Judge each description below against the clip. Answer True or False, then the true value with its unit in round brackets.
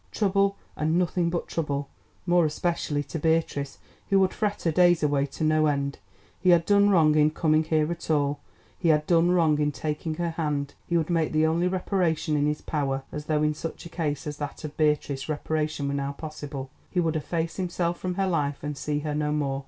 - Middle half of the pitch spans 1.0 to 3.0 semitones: True (2.6 semitones)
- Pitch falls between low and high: True (155 Hz)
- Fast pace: True (215 wpm)